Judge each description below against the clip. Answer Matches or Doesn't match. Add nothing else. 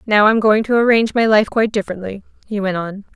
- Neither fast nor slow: Doesn't match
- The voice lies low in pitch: Doesn't match